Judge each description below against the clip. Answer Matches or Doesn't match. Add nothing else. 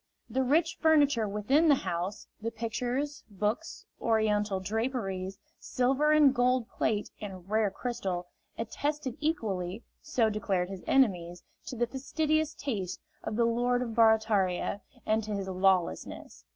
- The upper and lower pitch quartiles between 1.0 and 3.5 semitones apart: Doesn't match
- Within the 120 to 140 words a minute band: Matches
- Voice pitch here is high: Matches